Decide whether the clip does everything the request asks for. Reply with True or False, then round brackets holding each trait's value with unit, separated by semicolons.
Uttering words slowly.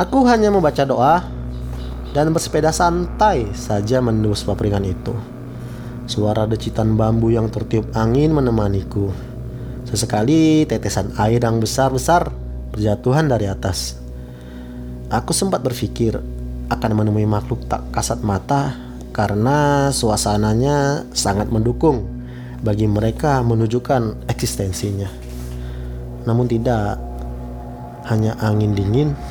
False (100 wpm)